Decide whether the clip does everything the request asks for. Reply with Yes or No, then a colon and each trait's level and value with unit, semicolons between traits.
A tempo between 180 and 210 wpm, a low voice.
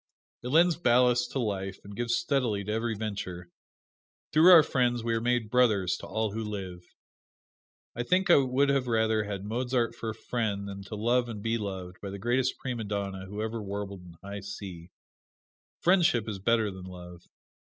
Yes: average, 185 wpm; low, 110 Hz